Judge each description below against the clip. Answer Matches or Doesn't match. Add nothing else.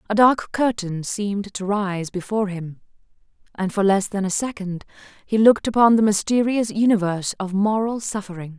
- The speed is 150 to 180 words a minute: Matches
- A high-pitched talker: Matches